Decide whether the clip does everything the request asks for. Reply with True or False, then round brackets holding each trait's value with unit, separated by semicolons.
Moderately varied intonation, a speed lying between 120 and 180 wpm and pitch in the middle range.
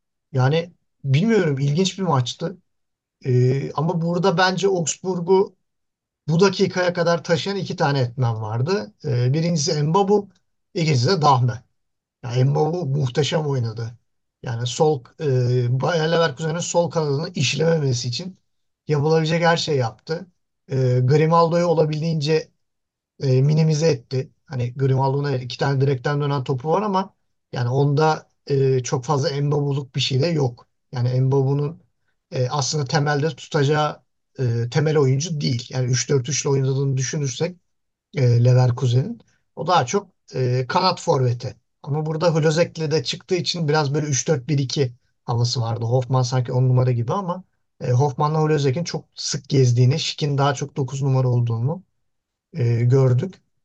True (4.3 semitones; 130 wpm; 145 Hz)